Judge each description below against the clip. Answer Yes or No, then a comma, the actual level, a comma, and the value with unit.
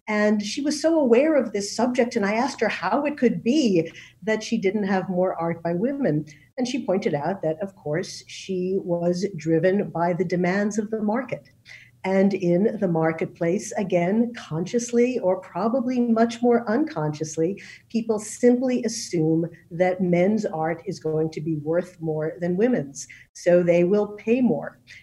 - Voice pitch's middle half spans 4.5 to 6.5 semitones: Yes, average, 5.2 semitones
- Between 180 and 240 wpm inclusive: No, average, 170 wpm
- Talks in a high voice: Yes, high, 195 Hz